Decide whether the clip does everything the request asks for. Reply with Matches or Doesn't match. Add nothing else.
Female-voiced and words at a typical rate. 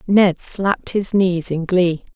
Matches